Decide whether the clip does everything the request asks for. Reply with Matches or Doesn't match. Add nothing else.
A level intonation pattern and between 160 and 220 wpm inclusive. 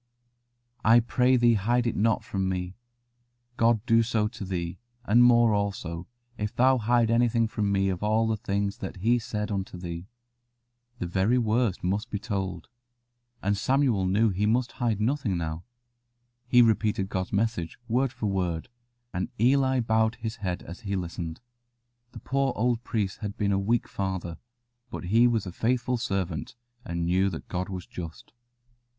Doesn't match